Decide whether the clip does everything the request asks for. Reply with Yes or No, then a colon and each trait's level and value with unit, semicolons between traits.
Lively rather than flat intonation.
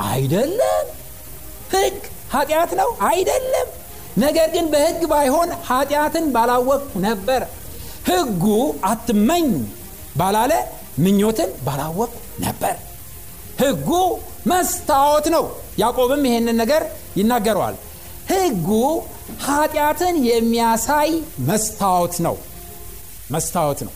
Yes: wide, 8.1 semitones